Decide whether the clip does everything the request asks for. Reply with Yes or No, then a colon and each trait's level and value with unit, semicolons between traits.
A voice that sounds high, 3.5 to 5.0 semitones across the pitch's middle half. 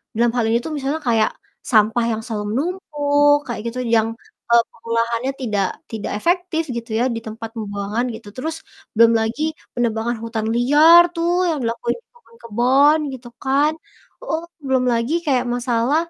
Yes: high, 240 Hz; average, 4.3 semitones